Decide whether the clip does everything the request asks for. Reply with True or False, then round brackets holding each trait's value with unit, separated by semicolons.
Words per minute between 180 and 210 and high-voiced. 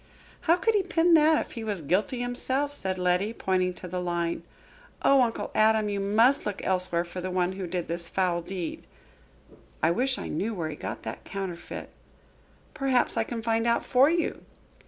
True (190 wpm; 200 Hz)